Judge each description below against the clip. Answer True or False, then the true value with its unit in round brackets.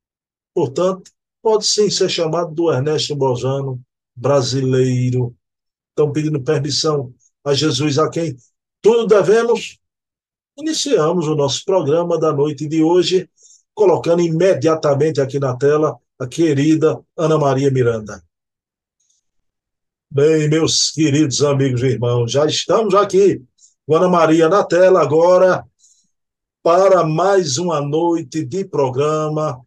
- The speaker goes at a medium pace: False (115 wpm)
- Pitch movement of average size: True (3.9 semitones)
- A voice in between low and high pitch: True (155 Hz)